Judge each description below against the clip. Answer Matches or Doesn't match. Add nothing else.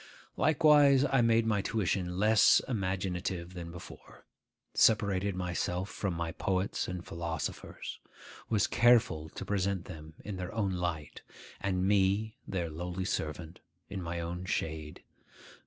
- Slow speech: Matches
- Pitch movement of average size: Matches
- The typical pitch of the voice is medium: Doesn't match